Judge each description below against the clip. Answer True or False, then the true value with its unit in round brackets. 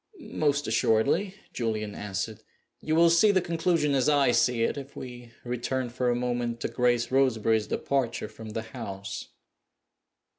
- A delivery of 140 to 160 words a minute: True (150 wpm)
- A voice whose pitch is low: True (125 Hz)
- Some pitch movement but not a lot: True (3.9 semitones)